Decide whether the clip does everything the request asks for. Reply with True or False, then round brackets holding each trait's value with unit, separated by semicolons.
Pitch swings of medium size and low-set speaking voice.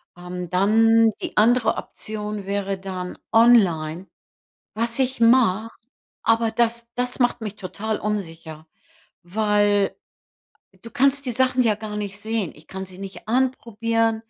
False (3.1 semitones; 215 Hz)